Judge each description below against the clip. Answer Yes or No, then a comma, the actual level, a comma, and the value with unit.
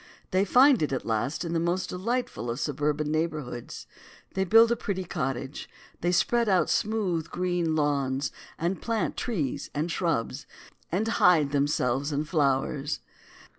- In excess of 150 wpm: No, average, 145 wpm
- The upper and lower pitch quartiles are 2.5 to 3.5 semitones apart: No, average, 4.8 semitones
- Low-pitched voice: No, medium, 165 Hz